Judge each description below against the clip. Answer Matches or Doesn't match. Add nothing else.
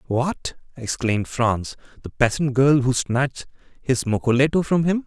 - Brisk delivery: Doesn't match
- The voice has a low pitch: Matches